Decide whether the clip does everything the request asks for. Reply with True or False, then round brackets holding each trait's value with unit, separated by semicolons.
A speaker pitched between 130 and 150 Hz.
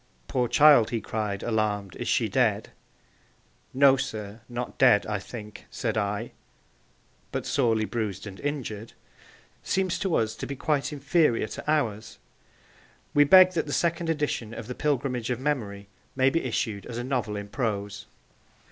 False (120 Hz)